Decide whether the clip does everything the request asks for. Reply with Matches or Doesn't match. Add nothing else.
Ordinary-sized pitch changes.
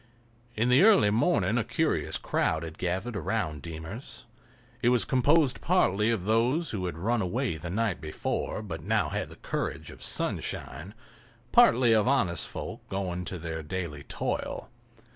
Doesn't match